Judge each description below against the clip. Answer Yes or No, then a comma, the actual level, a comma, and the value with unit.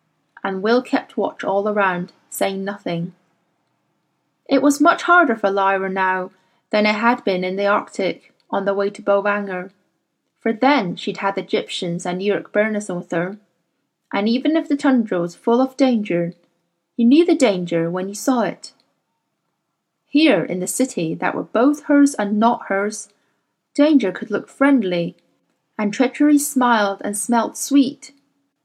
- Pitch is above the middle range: Yes, high, 210 Hz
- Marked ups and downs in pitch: Yes, wide, 6.1 semitones